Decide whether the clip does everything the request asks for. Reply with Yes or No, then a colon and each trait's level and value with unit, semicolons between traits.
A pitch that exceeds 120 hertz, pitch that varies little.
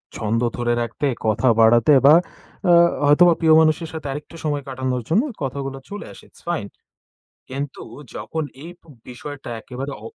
No: medium, 140 Hz; average, 4.0 semitones